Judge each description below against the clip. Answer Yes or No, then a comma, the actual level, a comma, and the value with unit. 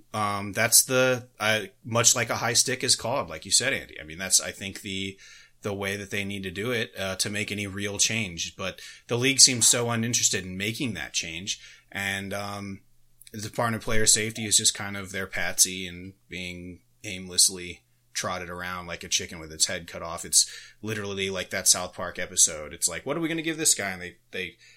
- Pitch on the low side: Yes, low, 100 Hz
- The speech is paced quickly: Yes, fast, 220 wpm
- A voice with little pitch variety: No, average, 3.4 semitones